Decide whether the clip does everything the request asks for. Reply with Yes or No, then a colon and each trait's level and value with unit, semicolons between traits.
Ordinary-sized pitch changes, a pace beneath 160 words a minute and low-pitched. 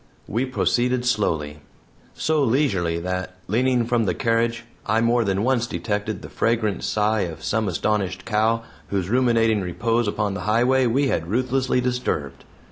Yes: average, 3.8 semitones; average, 150 wpm; low, 115 Hz